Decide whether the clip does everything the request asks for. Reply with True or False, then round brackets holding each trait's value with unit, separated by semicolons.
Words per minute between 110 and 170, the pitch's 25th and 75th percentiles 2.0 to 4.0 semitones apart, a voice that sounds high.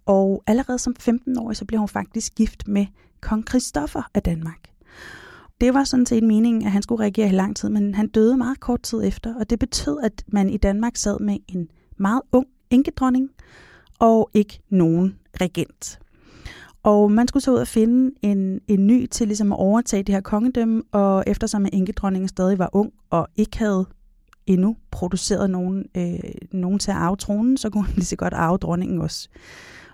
False (190 wpm; 3.2 semitones; 210 Hz)